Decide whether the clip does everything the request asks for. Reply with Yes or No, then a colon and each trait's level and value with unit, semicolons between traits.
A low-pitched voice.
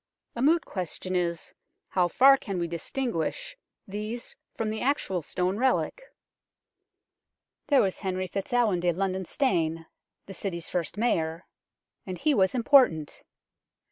No: high, 190 Hz